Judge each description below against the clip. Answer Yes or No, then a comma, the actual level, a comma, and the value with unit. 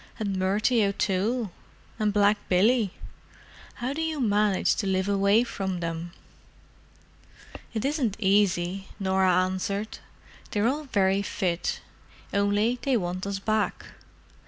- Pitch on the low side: No, high, 200 Hz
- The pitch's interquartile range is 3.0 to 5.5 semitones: No, narrow, 2.5 semitones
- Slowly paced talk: Yes, slow, 120 wpm